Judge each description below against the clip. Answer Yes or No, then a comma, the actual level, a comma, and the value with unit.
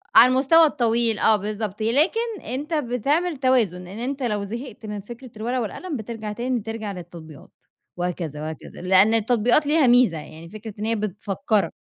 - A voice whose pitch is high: Yes, high, 225 Hz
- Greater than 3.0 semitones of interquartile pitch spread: Yes, average, 4.2 semitones